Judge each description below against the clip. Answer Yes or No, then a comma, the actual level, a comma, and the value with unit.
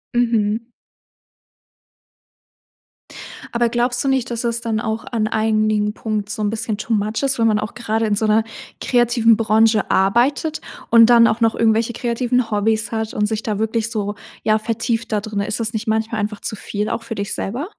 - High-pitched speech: Yes, high, 220 Hz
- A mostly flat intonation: Yes, narrow, 1.5 semitones